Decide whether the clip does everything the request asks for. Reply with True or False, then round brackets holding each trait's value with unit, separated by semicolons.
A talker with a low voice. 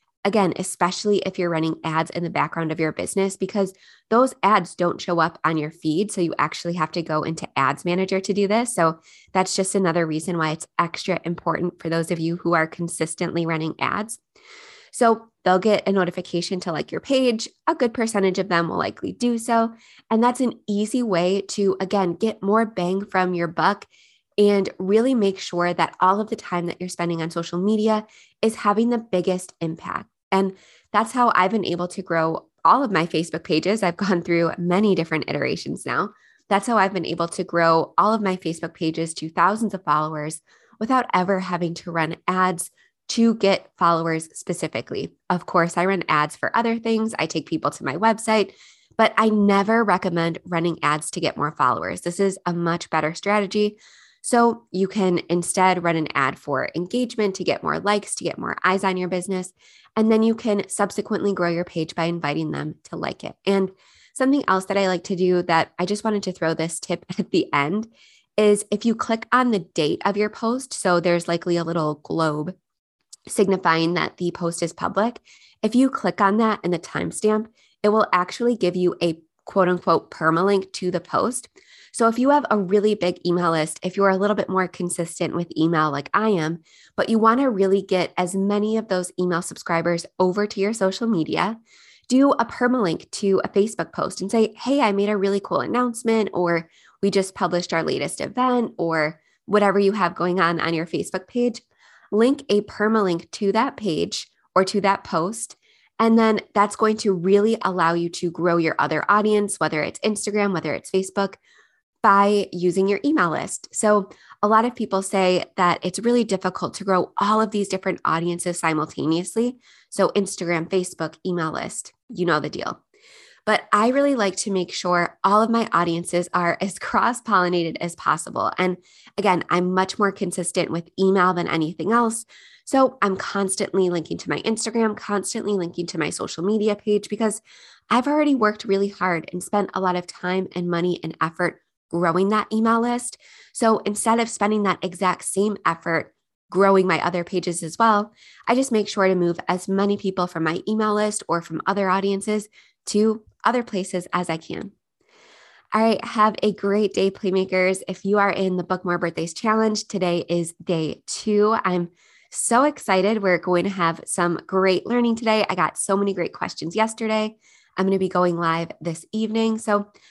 False (190 Hz)